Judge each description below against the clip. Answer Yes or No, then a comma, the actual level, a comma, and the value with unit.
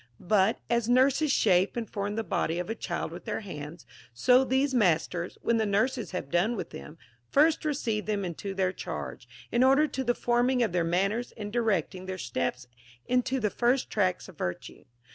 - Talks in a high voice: Yes, high, 215 Hz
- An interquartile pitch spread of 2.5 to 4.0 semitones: No, average, 5.3 semitones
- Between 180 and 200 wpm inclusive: Yes, average, 190 wpm